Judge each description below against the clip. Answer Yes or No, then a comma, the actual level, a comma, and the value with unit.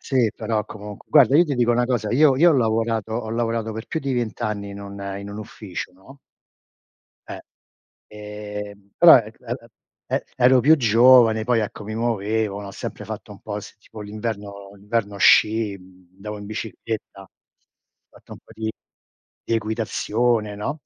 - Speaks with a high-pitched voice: No, low, 110 Hz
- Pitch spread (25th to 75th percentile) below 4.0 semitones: Yes, narrow, 2.6 semitones